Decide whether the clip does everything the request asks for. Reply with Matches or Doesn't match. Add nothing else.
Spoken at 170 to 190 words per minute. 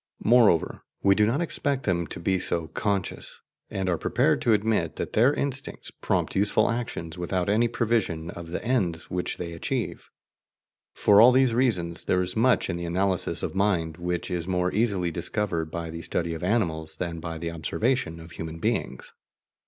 Matches